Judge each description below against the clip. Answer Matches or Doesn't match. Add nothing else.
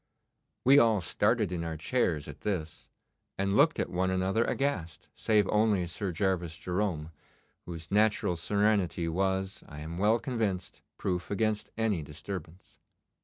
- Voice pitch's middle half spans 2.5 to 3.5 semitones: Doesn't match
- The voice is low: Matches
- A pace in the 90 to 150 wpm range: Matches